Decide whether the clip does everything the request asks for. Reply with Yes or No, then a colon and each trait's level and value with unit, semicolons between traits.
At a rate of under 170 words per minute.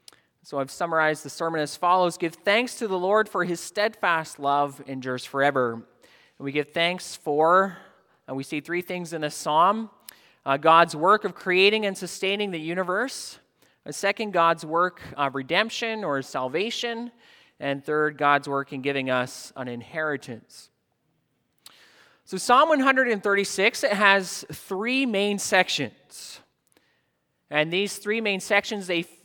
Yes: average, 145 wpm